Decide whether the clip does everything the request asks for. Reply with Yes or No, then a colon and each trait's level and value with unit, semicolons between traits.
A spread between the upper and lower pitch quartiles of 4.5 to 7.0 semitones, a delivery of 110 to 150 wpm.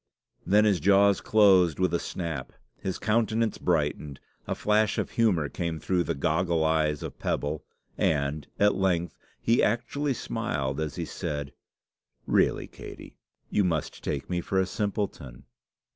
Yes: average, 5.2 semitones; average, 145 wpm